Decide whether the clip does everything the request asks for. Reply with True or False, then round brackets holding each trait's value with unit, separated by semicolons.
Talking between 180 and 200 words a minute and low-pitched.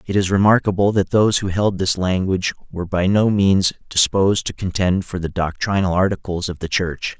True (190 wpm; 95 Hz)